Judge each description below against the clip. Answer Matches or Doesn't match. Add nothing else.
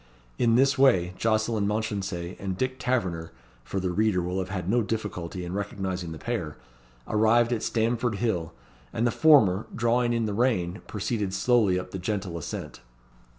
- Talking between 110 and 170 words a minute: Matches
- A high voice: Doesn't match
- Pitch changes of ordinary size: Matches